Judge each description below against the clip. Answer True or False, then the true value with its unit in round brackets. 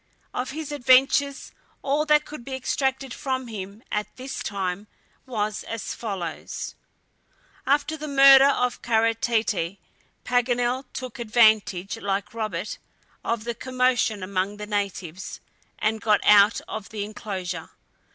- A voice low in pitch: False (230 Hz)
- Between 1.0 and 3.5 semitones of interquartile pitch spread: False (4.1 semitones)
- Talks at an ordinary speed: False (130 wpm)